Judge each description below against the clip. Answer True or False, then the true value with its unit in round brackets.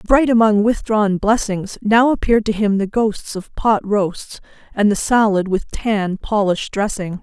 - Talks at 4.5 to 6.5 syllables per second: False (4.1 syllables/s)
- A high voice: True (210 Hz)